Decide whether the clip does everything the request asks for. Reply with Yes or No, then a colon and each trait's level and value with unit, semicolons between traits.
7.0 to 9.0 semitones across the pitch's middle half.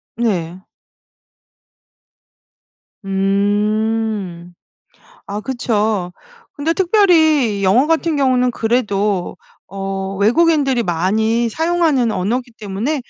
No: average, 5.3 semitones